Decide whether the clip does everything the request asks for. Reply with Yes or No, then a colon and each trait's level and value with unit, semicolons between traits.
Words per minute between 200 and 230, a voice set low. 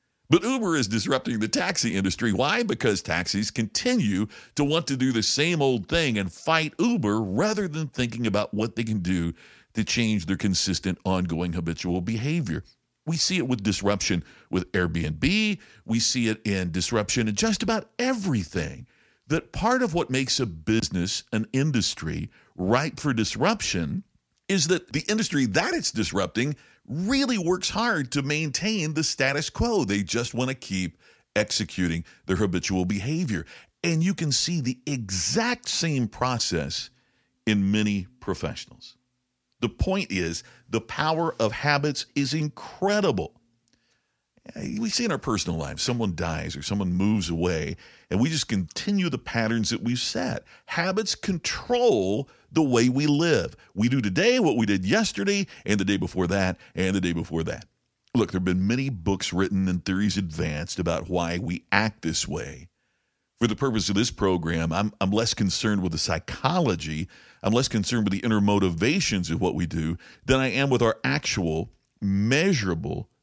No: average, 165 wpm; low, 115 Hz